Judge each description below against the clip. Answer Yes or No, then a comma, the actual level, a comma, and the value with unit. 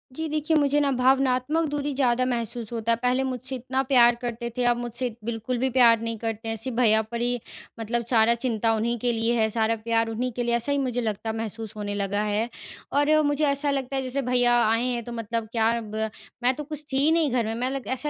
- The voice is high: Yes, high, 240 Hz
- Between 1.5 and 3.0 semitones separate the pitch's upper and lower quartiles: Yes, narrow, 2.6 semitones